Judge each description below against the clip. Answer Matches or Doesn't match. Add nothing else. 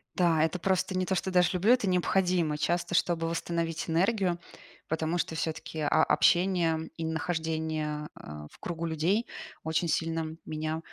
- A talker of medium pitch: Matches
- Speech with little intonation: Matches